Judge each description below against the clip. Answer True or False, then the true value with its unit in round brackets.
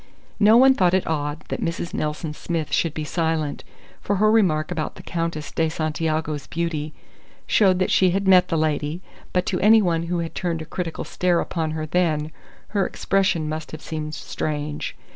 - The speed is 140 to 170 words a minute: False (185 wpm)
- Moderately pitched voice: True (165 Hz)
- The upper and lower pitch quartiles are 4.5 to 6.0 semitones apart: False (2.9 semitones)